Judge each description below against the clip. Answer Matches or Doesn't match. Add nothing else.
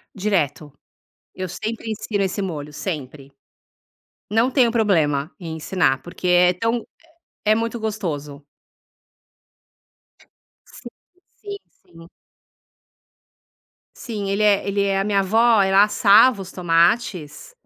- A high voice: Matches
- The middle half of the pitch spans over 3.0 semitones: Matches